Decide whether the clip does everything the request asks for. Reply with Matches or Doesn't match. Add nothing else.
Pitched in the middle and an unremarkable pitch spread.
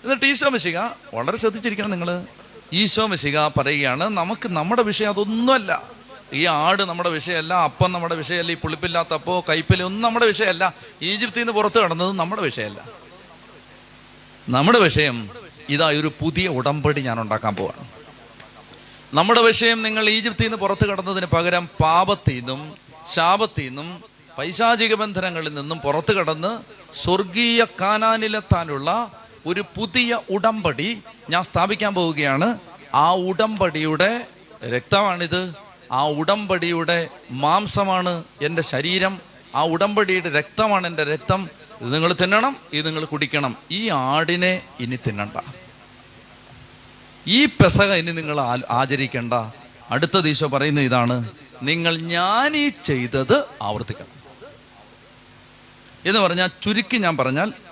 Doesn't match